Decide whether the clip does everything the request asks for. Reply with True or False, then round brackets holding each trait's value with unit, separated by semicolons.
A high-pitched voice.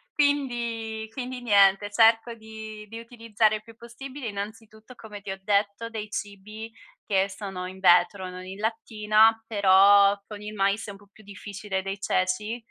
True (215 Hz)